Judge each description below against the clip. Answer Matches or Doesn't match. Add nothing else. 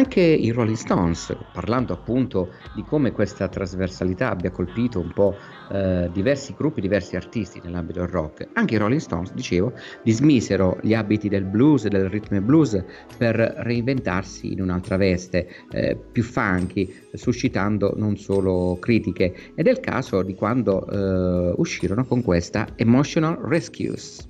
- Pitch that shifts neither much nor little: Matches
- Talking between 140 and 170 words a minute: Matches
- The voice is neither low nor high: Doesn't match